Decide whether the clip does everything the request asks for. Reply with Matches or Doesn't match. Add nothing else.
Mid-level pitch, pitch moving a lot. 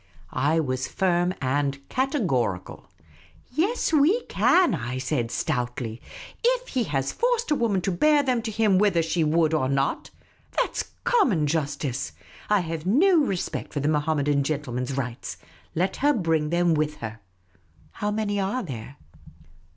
Matches